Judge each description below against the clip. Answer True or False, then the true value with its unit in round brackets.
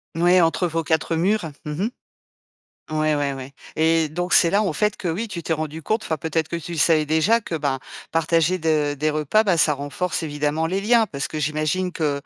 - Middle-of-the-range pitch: True (160 Hz)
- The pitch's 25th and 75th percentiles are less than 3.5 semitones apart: True (2.8 semitones)